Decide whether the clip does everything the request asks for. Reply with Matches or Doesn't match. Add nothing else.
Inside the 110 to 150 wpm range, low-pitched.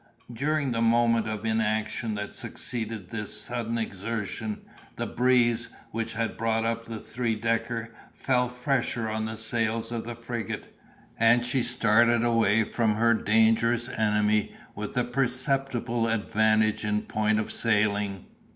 Matches